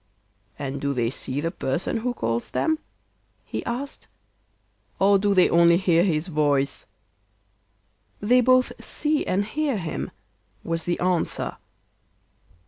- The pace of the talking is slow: Yes, slow, 130 wpm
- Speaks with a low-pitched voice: No, medium, 175 Hz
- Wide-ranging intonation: Yes, wide, 7.1 semitones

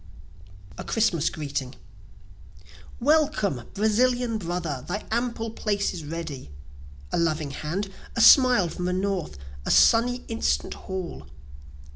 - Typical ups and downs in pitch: No, wide, 5.9 semitones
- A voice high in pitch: Yes, high, 195 Hz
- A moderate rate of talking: No, slow, 115 wpm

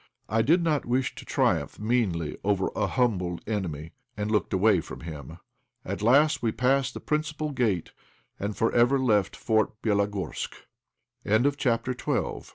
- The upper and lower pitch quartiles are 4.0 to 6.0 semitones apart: Yes, average, 4.4 semitones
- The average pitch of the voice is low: Yes, low, 110 Hz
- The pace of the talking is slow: No, average, 150 wpm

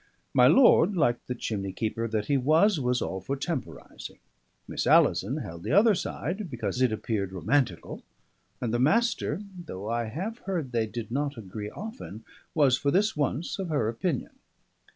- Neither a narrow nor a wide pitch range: No, wide, 7.0 semitones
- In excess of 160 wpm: Yes, average, 170 wpm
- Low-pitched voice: Yes, low, 130 Hz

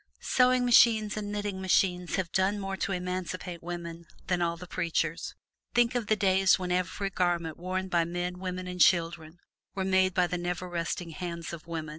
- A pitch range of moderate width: No, narrow, 1.9 semitones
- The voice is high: No, medium, 180 Hz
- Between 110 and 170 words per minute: No, average, 185 wpm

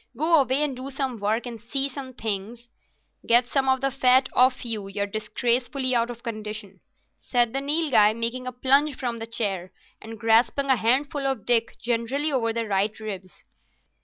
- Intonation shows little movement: No, average, 3.2 semitones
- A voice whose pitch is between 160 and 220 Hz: No, high, 240 Hz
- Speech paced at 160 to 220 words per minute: Yes, average, 180 wpm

